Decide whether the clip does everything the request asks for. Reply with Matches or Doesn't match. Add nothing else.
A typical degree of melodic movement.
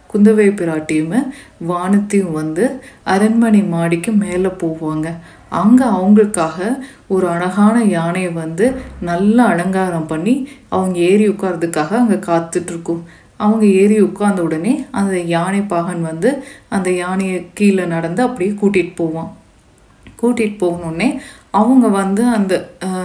Matches